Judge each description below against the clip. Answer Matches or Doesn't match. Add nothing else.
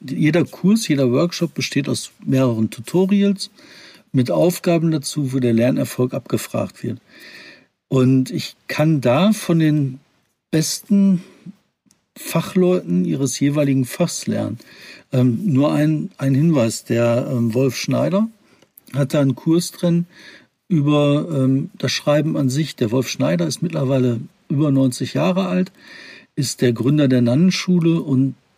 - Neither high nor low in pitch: Matches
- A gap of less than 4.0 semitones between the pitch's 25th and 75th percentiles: Doesn't match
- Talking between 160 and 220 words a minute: Doesn't match